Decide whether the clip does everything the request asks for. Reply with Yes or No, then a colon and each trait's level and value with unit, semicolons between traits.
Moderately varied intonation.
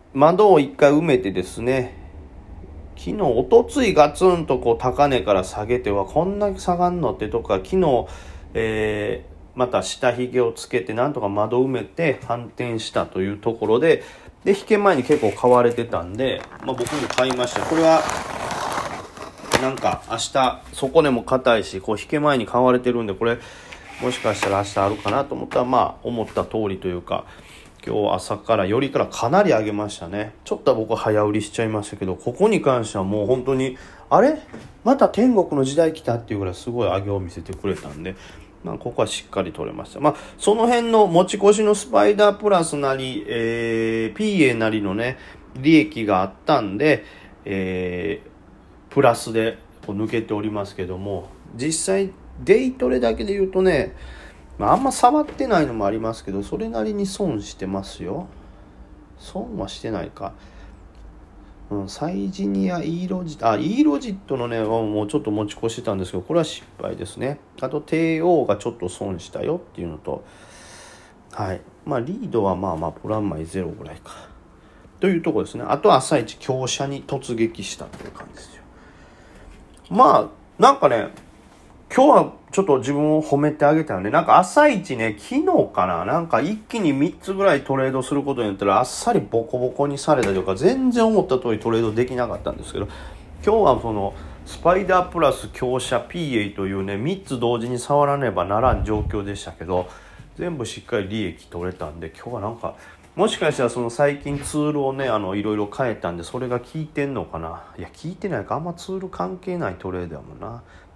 No: wide, 7.6 semitones